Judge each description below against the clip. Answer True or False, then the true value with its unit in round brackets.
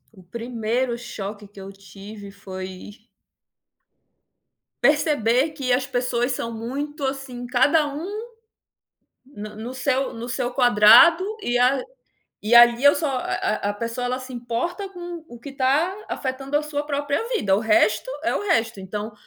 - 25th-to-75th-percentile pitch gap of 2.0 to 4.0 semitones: False (4.5 semitones)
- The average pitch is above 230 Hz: True (245 Hz)